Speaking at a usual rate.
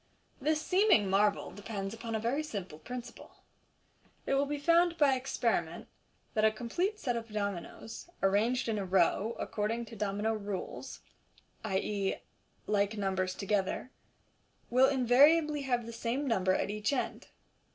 Yes: average, 145 wpm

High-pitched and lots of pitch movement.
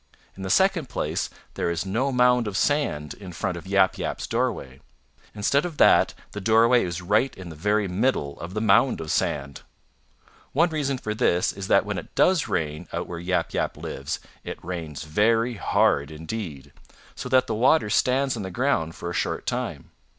No: low, 105 Hz; wide, 6.6 semitones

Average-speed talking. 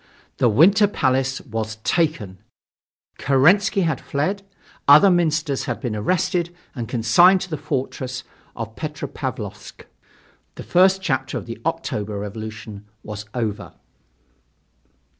No: slow, 115 wpm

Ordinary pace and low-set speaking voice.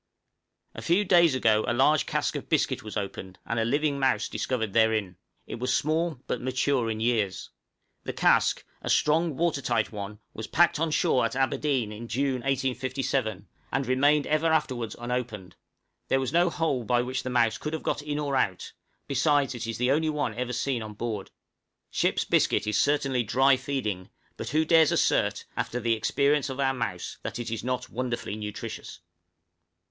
Yes: average, 185 wpm; low, 130 Hz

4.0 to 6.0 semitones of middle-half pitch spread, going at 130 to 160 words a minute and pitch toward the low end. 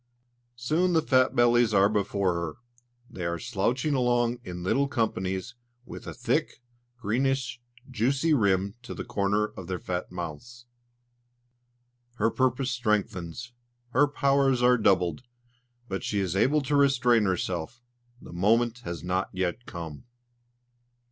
Yes: average, 5.2 semitones; slow, 135 wpm; low, 115 Hz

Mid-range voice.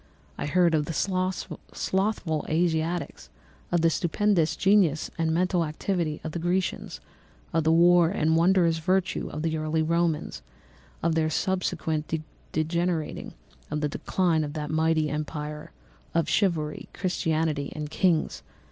Yes: medium, 165 Hz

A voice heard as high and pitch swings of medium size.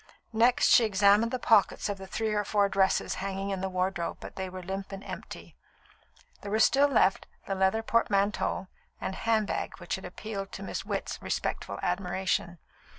No: high, 195 Hz; narrow, 2.2 semitones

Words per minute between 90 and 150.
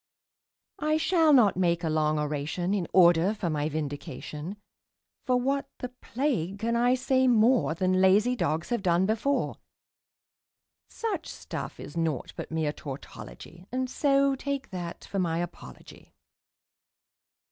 Yes: slow, 135 wpm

